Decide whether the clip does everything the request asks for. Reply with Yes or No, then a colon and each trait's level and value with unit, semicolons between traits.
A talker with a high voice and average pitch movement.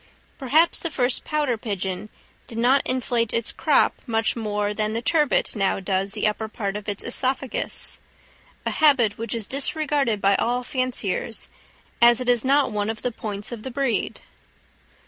Yes: high, 230 Hz; average, 3.6 semitones